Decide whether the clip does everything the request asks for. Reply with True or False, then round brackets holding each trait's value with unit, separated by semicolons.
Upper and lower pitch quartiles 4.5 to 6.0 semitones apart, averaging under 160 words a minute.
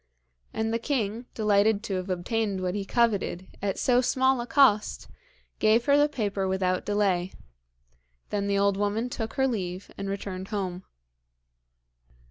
False (3.2 semitones; 150 wpm)